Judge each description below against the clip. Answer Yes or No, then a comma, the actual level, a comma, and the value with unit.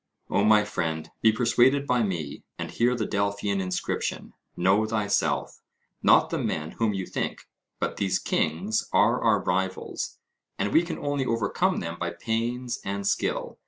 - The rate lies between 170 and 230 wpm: No, average, 160 wpm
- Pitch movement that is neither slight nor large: Yes, average, 3.8 semitones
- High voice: No, low, 105 Hz